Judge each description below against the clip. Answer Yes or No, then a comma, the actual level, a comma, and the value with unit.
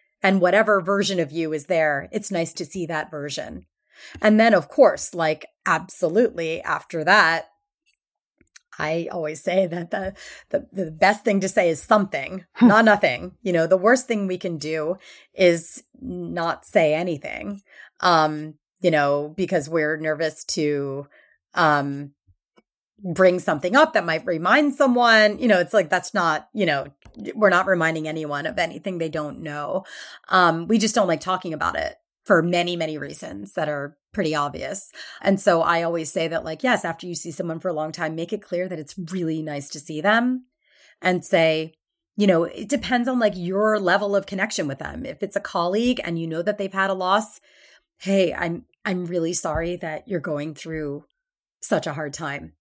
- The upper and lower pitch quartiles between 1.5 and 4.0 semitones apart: No, average, 4.4 semitones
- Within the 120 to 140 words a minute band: No, average, 185 wpm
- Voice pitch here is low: No, medium, 175 Hz